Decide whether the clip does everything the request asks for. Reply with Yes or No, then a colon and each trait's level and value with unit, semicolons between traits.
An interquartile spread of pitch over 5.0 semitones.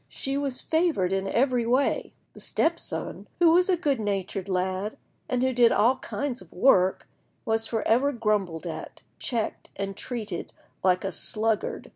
Yes: wide, 5.6 semitones